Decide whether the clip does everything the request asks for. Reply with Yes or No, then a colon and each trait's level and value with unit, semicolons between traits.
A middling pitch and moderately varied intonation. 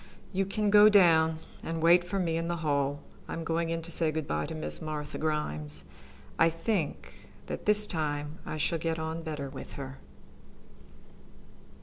No: medium, 160 Hz; narrow, 2.3 semitones